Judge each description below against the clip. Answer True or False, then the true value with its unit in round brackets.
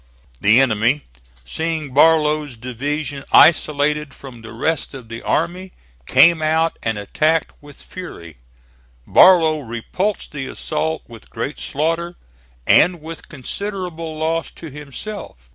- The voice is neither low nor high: True (150 Hz)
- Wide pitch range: False (4.2 semitones)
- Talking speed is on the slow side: True (120 wpm)